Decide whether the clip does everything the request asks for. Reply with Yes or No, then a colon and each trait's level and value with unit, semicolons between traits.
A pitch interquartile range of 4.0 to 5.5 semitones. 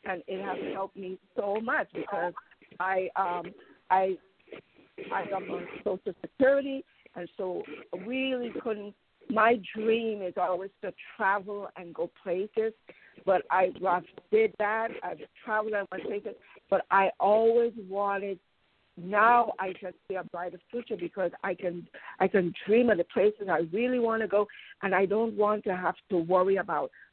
No: average, 3.6 semitones